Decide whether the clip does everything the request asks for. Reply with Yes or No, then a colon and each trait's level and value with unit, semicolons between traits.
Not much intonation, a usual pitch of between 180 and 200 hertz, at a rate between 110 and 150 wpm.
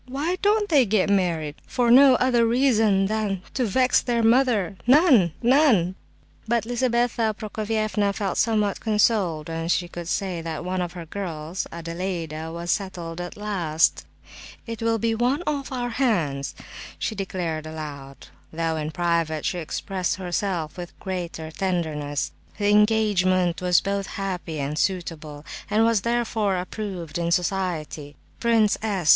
No: average, 5.1 semitones; high, 190 Hz; average, 140 wpm